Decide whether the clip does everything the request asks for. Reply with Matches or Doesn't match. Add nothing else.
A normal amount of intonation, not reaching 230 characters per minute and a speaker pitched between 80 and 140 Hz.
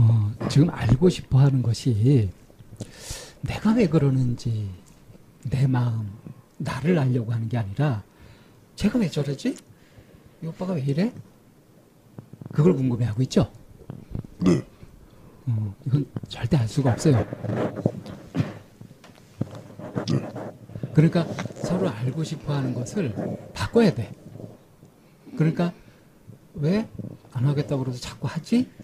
Matches